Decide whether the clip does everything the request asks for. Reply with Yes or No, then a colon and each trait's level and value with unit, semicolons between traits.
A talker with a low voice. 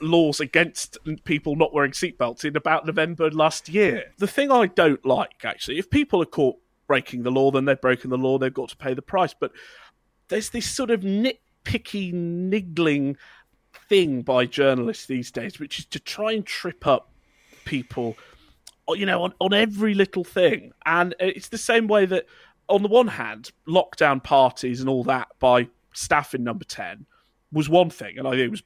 No: medium, 160 Hz